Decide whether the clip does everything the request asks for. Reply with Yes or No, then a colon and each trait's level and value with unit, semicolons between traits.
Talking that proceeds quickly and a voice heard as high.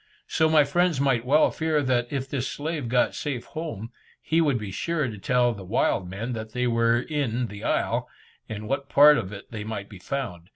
No: fast, 215 wpm; low, 125 Hz